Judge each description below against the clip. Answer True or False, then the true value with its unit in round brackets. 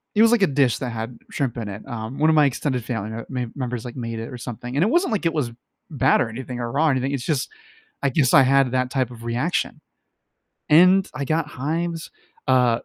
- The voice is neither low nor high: False (130 Hz)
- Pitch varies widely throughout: False (4.1 semitones)